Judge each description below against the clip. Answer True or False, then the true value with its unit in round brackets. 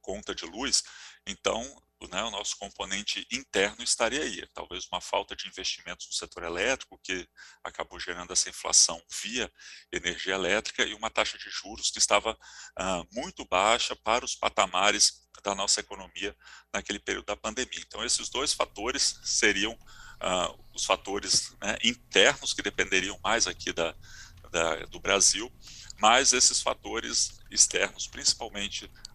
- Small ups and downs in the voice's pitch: False (5.6 semitones)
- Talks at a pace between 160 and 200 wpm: False (145 wpm)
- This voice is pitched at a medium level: False (110 Hz)